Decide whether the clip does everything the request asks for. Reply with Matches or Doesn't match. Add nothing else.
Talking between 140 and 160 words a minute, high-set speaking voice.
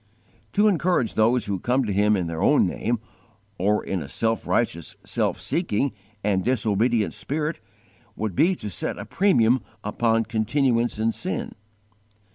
Doesn't match